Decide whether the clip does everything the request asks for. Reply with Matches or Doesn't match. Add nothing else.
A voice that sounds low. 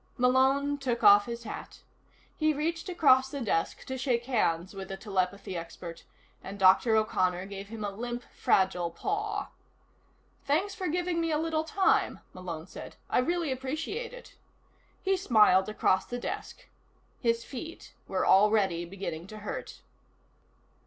Doesn't match